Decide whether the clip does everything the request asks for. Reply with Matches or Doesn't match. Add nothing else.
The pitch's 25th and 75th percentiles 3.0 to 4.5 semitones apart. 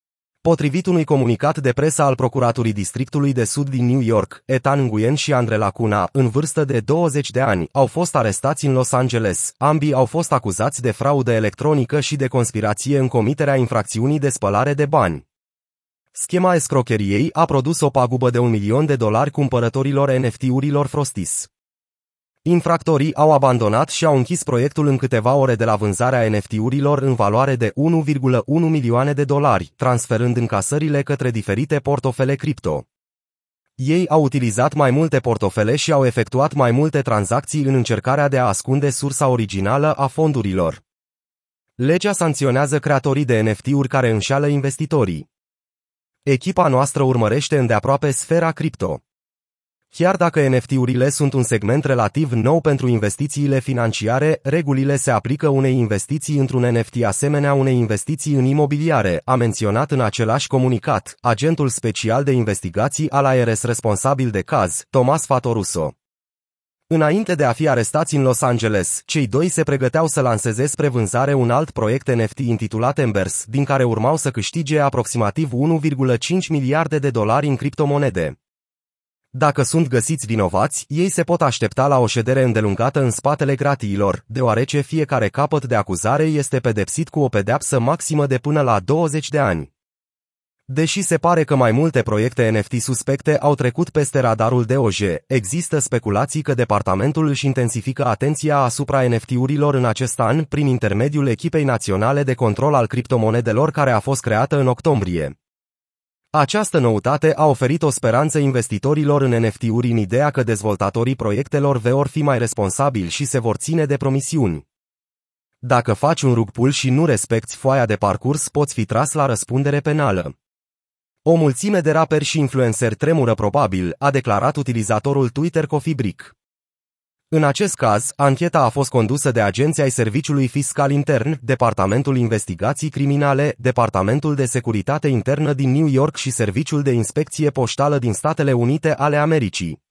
Matches